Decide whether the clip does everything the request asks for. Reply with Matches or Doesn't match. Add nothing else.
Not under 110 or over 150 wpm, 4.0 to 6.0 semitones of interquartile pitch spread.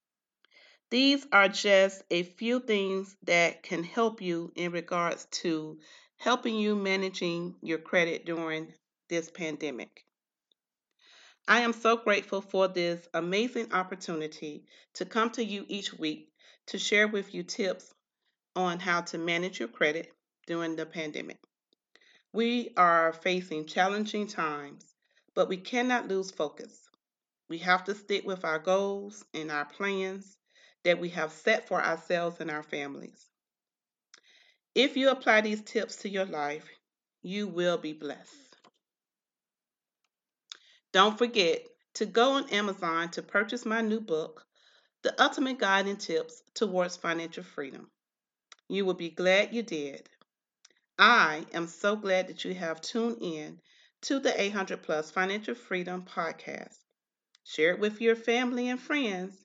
Matches